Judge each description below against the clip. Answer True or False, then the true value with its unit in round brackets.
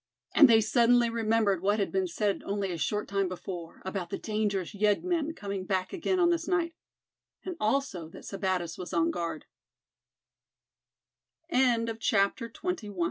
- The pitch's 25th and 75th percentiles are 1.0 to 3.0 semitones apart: False (4.1 semitones)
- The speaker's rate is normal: True (160 wpm)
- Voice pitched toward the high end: True (210 Hz)